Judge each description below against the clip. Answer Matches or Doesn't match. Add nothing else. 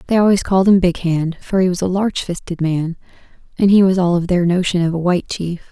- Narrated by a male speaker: Doesn't match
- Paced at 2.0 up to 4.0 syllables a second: Doesn't match